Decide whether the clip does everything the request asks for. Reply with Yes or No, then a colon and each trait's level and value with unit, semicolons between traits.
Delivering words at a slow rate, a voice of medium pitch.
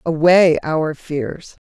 Yes: slow, 110 wpm; medium, 160 Hz